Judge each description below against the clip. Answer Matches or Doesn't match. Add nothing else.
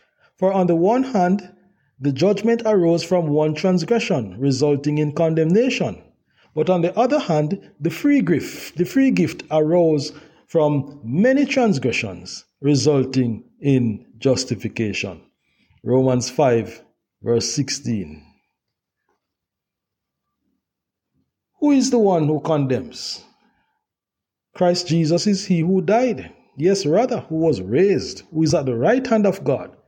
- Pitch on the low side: Doesn't match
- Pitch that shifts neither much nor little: Doesn't match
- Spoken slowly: Matches